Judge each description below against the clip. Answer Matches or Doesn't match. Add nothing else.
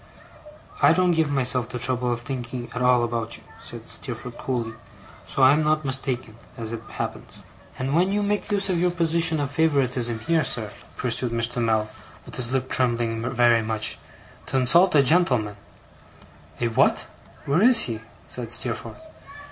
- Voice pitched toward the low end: Matches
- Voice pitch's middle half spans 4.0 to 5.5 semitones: Matches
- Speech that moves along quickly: Doesn't match